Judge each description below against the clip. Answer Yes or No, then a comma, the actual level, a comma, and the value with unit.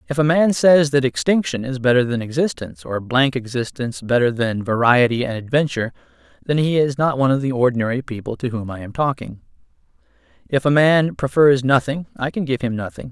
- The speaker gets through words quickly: No, average, 190 wpm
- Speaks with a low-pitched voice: Yes, low, 130 Hz